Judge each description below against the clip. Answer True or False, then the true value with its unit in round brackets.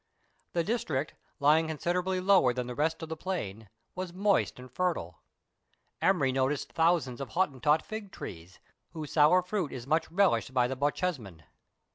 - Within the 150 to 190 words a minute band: True (165 wpm)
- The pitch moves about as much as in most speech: False (5.9 semitones)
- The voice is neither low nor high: True (155 Hz)